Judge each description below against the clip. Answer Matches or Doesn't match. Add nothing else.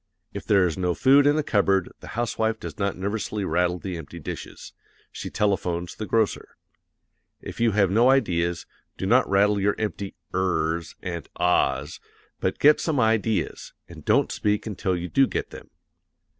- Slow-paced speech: Doesn't match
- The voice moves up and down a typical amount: Matches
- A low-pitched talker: Matches